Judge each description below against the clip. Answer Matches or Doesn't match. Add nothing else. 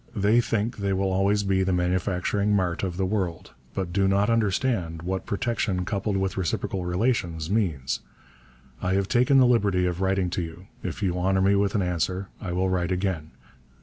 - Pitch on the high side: Doesn't match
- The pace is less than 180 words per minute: Doesn't match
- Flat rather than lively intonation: Matches